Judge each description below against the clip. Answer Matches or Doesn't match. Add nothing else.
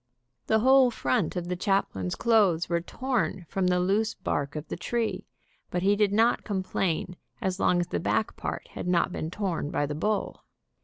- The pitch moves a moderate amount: Matches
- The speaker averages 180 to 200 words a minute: Matches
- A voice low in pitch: Doesn't match